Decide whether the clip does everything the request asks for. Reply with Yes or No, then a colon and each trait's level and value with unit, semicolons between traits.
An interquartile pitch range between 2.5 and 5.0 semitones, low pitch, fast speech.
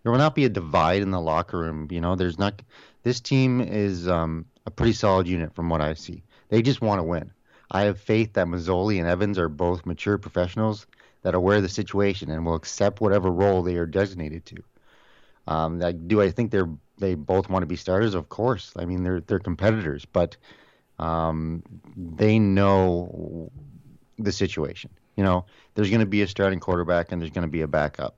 Yes: average, 3.3 semitones; very low, 95 Hz; fast, 210 wpm